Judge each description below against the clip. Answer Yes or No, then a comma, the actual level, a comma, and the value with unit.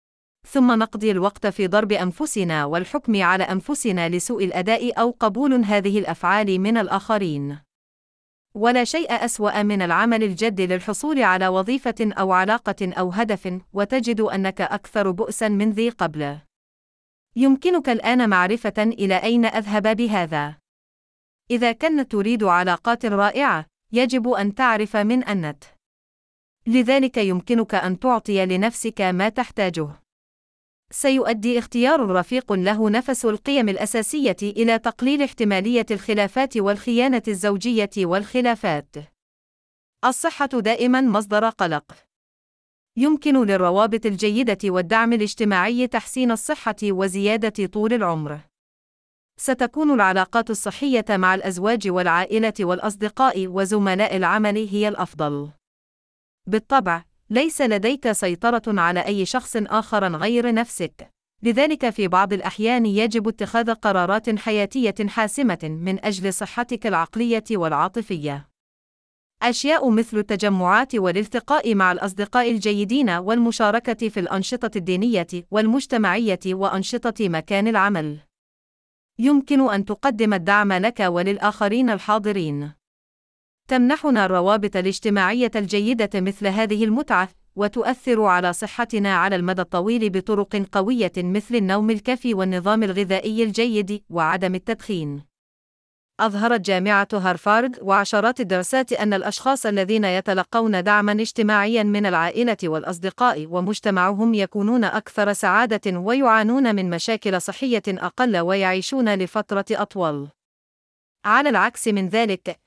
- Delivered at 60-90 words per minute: No, average, 105 wpm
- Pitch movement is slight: No, average, 3.6 semitones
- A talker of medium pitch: No, high, 210 Hz